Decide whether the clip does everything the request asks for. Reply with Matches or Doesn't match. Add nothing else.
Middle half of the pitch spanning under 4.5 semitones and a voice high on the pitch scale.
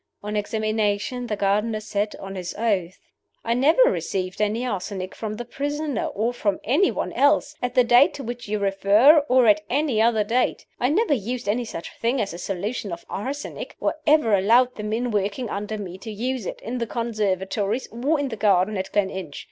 Matches